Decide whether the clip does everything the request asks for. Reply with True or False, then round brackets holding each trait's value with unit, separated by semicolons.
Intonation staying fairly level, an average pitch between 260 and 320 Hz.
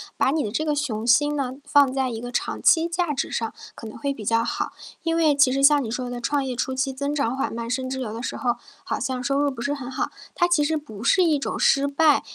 False (3.1 semitones; 270 Hz)